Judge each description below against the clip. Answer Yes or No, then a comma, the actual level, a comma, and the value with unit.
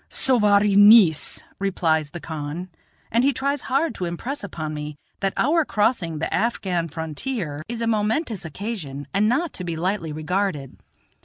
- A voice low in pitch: No, high, 195 Hz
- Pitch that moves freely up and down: Yes, wide, 6.3 semitones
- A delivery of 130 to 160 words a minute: Yes, average, 155 wpm